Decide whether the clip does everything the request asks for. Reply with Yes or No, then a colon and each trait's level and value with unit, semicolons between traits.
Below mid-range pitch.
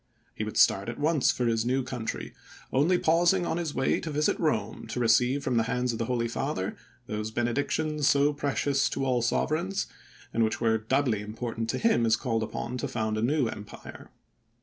Yes: low, 125 Hz